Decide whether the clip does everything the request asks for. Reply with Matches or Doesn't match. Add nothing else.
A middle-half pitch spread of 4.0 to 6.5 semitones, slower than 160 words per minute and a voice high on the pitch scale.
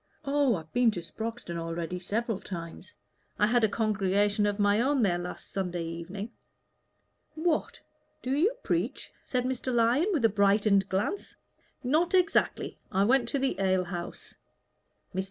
Matches